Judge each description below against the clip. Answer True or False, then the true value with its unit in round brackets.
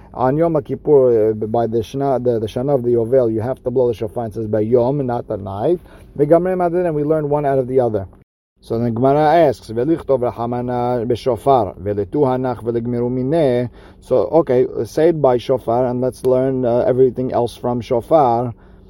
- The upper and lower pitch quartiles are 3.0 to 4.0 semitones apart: False (2.5 semitones)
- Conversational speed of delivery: True (165 wpm)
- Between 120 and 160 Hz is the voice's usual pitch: True (125 Hz)